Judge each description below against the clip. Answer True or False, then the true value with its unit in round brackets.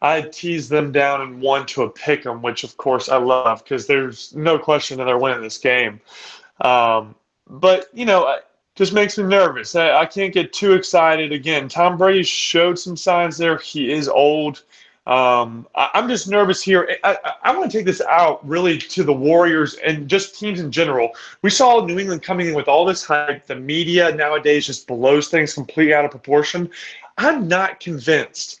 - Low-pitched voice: False (160 Hz)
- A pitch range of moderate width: True (4.6 semitones)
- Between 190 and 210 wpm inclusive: True (200 wpm)